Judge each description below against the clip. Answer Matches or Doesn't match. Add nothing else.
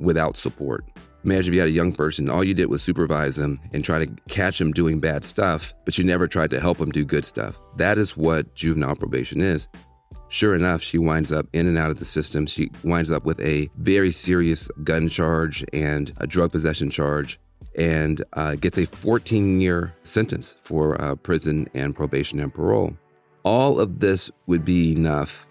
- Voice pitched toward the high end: Doesn't match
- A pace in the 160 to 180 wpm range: Doesn't match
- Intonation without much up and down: Doesn't match